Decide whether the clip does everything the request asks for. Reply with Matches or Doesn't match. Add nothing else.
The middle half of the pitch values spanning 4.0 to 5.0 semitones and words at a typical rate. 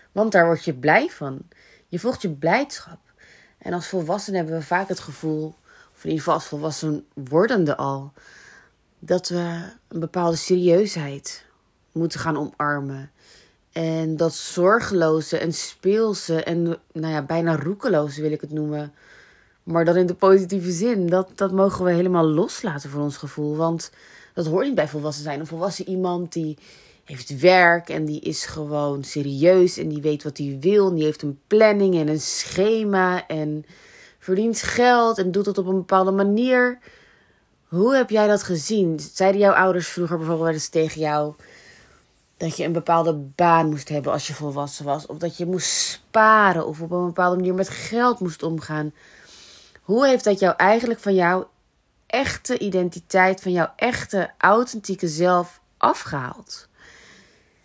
Doesn't match